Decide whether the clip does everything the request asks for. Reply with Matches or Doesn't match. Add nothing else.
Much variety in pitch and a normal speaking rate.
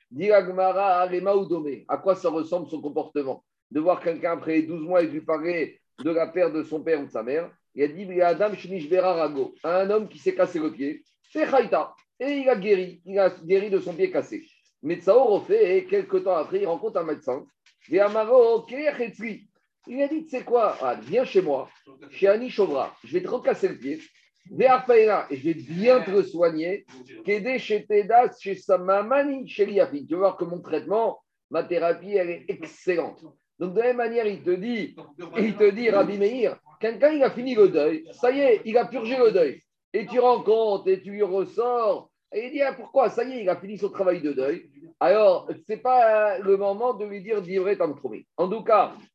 Matches